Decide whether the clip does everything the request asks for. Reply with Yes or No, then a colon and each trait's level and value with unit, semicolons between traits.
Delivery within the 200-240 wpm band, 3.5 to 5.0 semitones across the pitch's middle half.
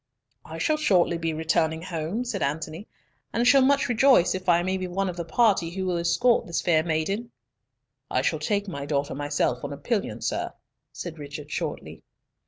No: average, 190 wpm; average, 4.4 semitones